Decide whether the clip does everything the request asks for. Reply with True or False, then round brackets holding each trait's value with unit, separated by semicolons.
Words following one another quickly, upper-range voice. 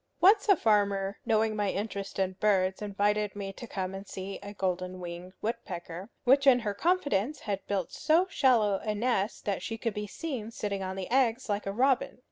False (195 wpm; 205 Hz)